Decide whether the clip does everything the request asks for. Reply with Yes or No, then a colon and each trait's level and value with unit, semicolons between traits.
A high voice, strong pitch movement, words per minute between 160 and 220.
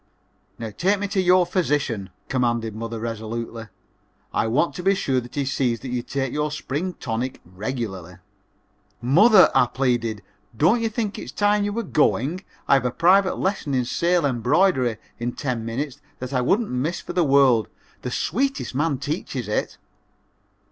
No: low, 135 Hz; wide, 7.2 semitones; average, 170 wpm